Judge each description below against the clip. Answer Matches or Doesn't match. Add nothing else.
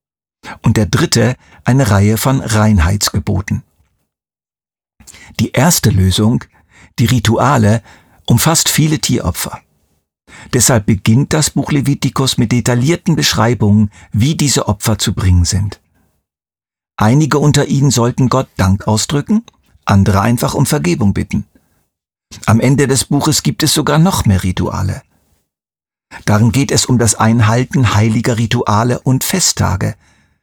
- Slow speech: Matches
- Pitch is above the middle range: Doesn't match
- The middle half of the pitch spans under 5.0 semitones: Doesn't match